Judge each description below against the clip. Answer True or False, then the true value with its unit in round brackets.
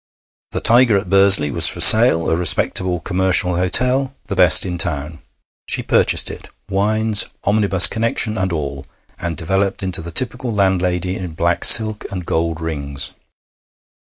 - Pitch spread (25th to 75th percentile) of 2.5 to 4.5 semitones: True (3.8 semitones)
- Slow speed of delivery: False (155 wpm)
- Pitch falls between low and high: False (95 Hz)